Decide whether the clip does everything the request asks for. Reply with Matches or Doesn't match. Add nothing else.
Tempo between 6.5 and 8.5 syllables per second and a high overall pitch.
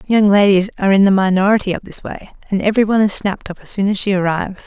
Matches